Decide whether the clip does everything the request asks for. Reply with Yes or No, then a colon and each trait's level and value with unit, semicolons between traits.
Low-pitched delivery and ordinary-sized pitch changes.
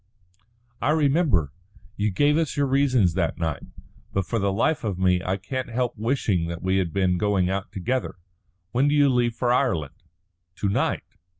No: low, 105 Hz; wide, 5.9 semitones